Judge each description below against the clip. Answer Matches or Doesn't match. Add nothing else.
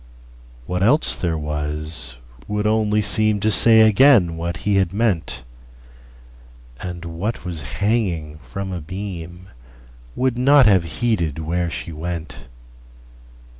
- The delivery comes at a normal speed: Doesn't match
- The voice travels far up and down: Matches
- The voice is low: Matches